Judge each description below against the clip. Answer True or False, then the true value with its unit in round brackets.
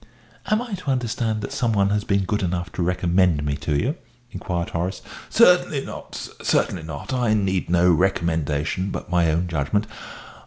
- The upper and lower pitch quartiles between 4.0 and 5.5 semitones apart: True (4.3 semitones)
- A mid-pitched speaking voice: False (95 Hz)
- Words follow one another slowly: False (180 wpm)